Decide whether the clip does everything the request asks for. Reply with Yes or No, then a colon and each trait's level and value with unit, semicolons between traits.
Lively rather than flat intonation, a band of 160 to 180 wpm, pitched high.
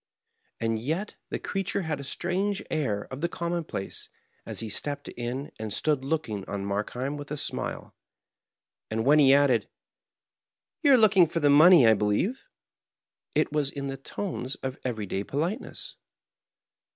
No: wide, 6.4 semitones; average, 165 wpm; medium, 140 Hz